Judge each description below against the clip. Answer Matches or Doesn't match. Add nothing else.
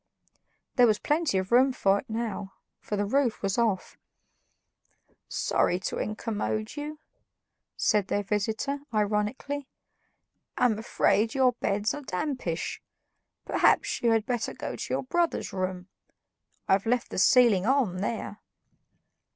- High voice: Matches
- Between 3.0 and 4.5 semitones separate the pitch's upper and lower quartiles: Matches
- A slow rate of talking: Matches